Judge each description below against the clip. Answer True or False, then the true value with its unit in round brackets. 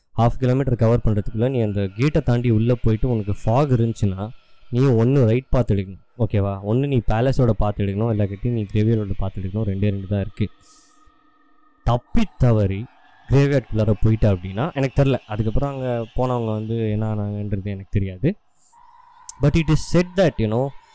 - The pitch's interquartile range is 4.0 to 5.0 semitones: True (4.4 semitones)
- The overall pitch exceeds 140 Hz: False (115 Hz)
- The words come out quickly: True (160 wpm)